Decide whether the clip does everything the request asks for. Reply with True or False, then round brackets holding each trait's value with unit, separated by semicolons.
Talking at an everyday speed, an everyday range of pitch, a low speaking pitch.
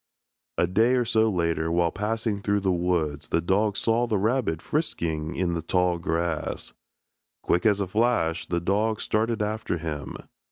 True (165 wpm; 4.7 semitones; 95 Hz)